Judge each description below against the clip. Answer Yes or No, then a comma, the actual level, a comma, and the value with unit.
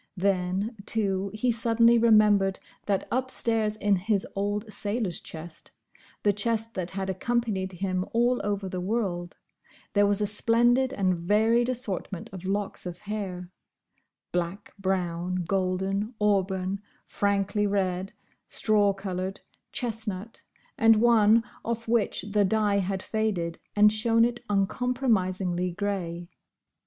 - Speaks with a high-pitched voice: Yes, high, 205 Hz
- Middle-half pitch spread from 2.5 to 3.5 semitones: Yes, average, 3.0 semitones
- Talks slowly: Yes, slow, 125 wpm